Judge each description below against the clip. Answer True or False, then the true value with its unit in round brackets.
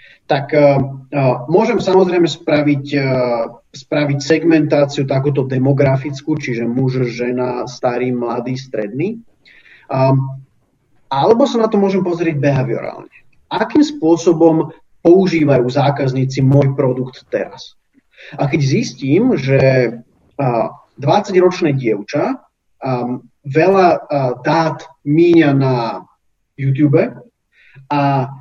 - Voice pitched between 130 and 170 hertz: True (140 Hz)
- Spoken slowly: True (100 wpm)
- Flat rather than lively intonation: False (3.7 semitones)